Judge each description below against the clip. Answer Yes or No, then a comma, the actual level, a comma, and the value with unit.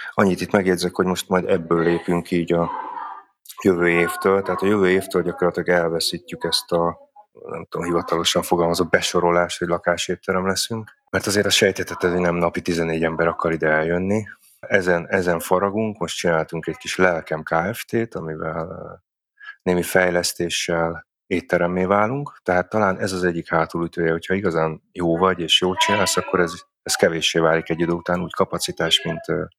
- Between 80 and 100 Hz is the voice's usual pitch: Yes, very low, 90 Hz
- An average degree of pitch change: No, narrow, 2.0 semitones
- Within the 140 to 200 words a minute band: Yes, fast, 155 wpm